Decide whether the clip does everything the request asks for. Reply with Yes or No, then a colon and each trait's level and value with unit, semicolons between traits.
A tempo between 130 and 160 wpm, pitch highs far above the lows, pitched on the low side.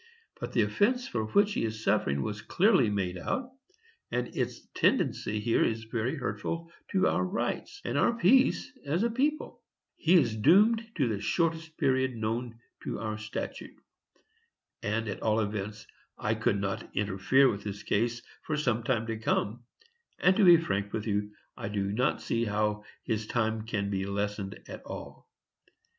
No: average, 170 wpm; wide, 7.3 semitones; low, 115 Hz